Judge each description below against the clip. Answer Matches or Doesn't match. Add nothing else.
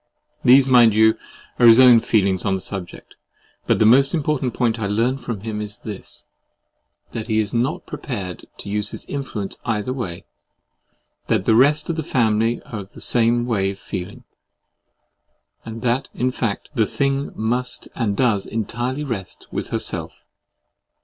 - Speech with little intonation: Doesn't match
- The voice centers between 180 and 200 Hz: Doesn't match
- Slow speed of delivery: Doesn't match